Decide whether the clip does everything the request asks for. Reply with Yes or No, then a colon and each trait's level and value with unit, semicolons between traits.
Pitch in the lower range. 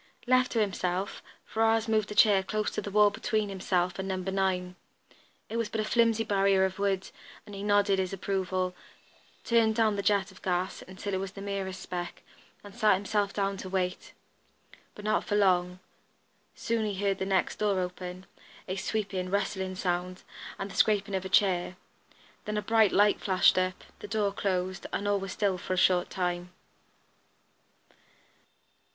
No: high, 195 Hz